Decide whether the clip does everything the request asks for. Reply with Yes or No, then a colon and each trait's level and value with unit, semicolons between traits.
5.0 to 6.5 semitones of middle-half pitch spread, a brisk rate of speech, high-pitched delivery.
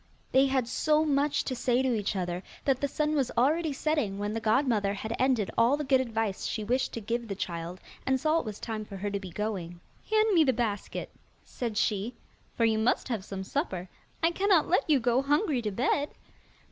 Yes: wide, 5.4 semitones; fast, 215 wpm; high, 240 Hz